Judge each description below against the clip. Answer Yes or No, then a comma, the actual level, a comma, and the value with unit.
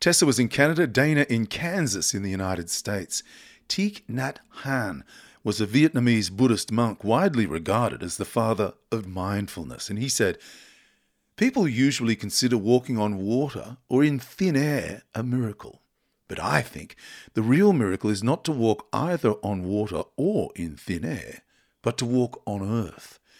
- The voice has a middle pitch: No, low, 115 Hz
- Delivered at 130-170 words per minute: Yes, average, 160 wpm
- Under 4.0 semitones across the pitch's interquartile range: No, average, 4.5 semitones